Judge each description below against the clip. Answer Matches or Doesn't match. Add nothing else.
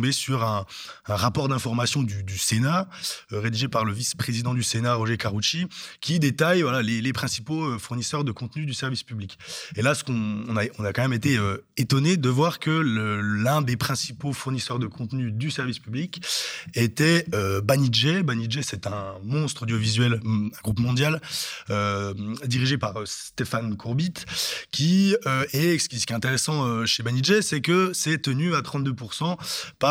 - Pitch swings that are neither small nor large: Matches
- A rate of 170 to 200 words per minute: Matches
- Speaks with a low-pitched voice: Matches